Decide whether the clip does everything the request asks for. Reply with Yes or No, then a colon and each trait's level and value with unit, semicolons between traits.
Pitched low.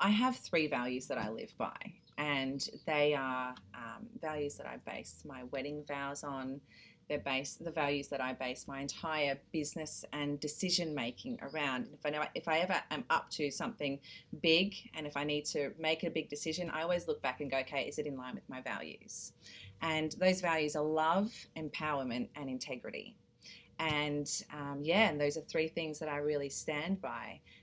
No: medium, 150 Hz